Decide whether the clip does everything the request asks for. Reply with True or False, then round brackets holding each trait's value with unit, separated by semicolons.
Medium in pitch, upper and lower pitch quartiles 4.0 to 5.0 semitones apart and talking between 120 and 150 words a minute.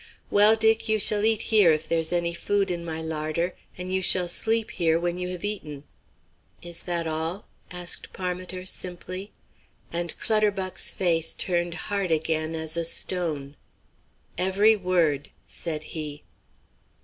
False (175 Hz; 2.8 semitones; 145 wpm)